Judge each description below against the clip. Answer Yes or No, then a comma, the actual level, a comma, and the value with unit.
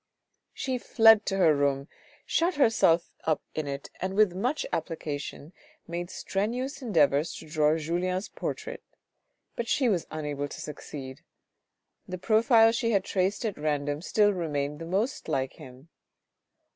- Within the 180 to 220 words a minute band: No, average, 145 wpm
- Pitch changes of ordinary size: No, wide, 6.9 semitones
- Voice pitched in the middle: Yes, medium, 175 Hz